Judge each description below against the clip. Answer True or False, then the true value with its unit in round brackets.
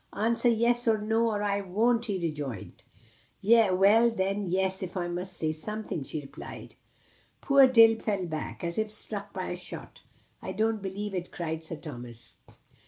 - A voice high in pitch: True (195 Hz)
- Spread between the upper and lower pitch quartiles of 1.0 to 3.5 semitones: False (4.2 semitones)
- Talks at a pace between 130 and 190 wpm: True (170 wpm)